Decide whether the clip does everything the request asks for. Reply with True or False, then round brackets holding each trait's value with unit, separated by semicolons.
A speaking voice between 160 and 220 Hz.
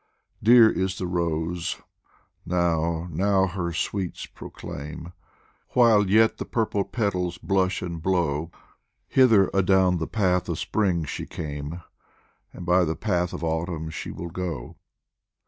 False (90 Hz)